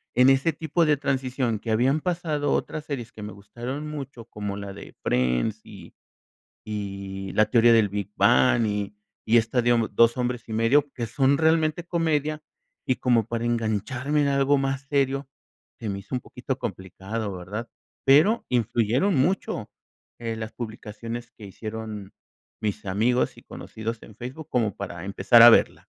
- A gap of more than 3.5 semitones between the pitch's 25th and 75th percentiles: Yes, average, 4.4 semitones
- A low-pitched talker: Yes, low, 120 Hz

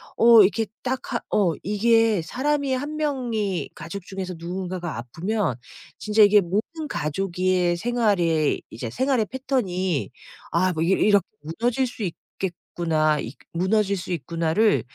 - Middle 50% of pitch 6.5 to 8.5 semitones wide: No, average, 5.1 semitones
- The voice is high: Yes, high, 195 Hz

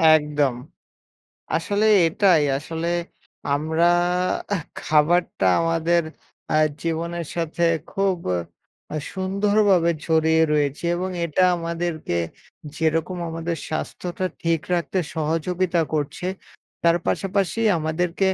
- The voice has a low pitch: No, medium, 165 Hz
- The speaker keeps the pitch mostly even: Yes, narrow, 2.2 semitones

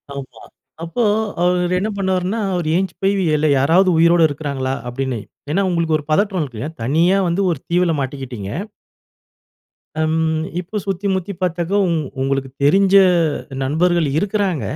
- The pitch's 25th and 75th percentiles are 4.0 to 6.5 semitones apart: Yes, average, 4.7 semitones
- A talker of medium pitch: Yes, medium, 170 Hz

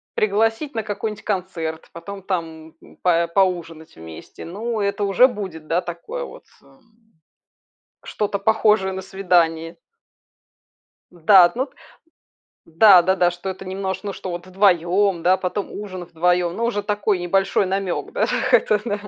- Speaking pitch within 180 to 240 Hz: Yes, high, 190 Hz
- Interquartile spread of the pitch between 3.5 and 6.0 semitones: No, average, 3.0 semitones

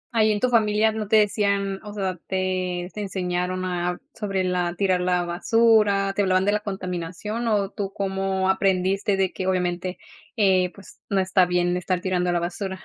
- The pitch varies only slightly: Yes, narrow, 2.0 semitones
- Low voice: No, high, 190 Hz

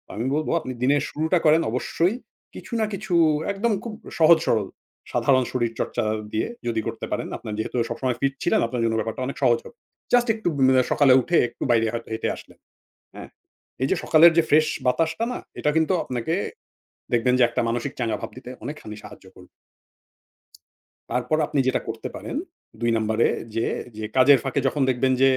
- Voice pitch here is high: No, low, 130 Hz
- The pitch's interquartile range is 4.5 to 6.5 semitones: Yes, average, 5.1 semitones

